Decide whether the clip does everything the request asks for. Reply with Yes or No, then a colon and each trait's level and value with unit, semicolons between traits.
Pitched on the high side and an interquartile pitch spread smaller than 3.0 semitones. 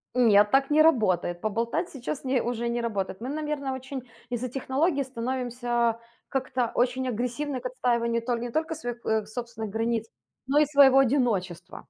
Yes: high, 245 Hz; narrow, 2.6 semitones